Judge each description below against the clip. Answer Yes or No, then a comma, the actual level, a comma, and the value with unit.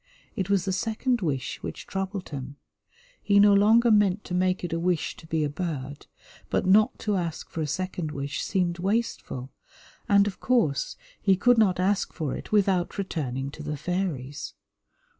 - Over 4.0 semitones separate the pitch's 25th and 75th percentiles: Yes, average, 4.7 semitones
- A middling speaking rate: Yes, average, 180 wpm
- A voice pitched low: No, medium, 185 Hz